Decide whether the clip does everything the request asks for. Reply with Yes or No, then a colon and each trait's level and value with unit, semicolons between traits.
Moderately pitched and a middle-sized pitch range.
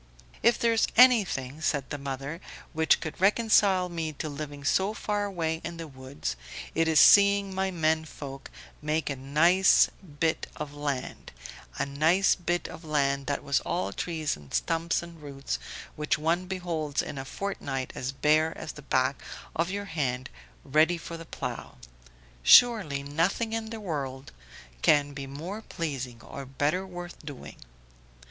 Yes: medium, 155 Hz; average, 4.3 semitones